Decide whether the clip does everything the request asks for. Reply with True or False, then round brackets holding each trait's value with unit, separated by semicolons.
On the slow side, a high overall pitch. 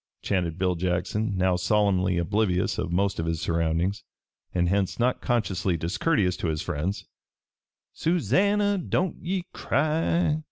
False (130 wpm; 95 Hz)